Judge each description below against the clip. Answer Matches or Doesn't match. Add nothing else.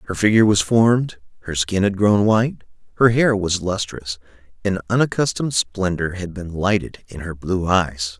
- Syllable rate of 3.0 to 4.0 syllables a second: Doesn't match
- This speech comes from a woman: Doesn't match